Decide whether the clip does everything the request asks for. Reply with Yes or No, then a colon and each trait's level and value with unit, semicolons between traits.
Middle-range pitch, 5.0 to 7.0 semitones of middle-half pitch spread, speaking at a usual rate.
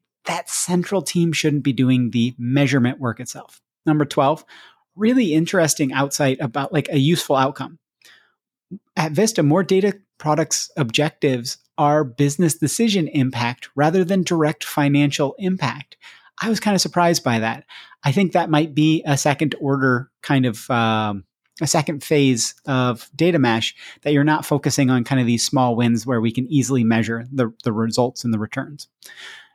No: medium, 145 Hz; average, 4.3 semitones; average, 160 wpm